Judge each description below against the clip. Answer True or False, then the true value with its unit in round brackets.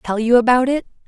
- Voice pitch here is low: False (245 Hz)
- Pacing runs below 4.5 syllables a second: False (5.9 syllables/s)